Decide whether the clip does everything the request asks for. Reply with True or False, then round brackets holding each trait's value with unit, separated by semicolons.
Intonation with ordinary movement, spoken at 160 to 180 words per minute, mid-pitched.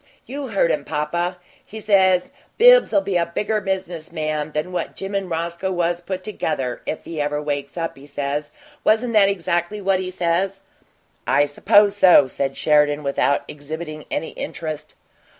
True (4.4 semitones; 165 wpm; 170 Hz)